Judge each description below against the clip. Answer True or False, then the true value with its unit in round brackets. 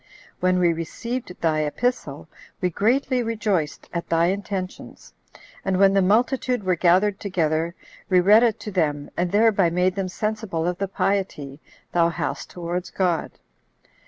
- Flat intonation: False (3.5 semitones)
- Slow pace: False (150 wpm)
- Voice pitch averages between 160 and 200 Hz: True (185 Hz)